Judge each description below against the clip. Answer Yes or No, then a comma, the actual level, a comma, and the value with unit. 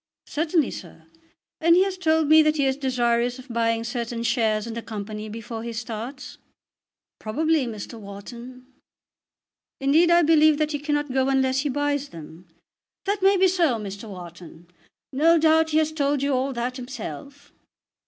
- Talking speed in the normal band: Yes, average, 165 wpm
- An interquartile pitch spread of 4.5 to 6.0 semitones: Yes, average, 5.1 semitones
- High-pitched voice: Yes, very high, 260 Hz